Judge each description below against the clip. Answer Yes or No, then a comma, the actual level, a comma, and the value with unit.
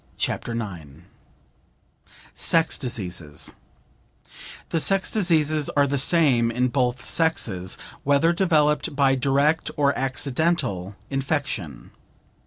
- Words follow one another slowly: Yes, slow, 95 wpm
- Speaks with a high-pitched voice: No, low, 135 Hz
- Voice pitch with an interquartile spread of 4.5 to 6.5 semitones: Yes, average, 5.2 semitones